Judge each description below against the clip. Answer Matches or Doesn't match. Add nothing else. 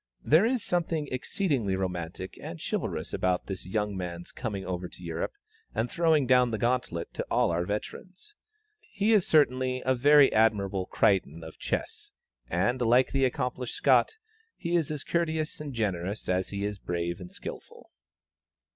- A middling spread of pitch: Doesn't match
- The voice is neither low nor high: Doesn't match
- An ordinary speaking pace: Matches